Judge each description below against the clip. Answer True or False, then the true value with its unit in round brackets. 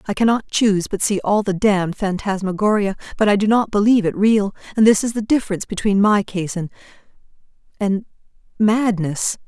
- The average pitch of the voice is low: False (205 Hz)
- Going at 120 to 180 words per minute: True (160 wpm)